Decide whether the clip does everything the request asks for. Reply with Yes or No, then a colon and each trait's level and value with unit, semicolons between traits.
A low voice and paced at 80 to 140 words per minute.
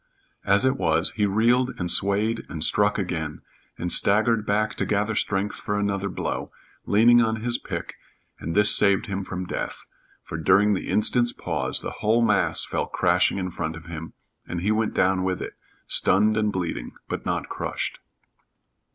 No: low, 100 Hz; average, 175 wpm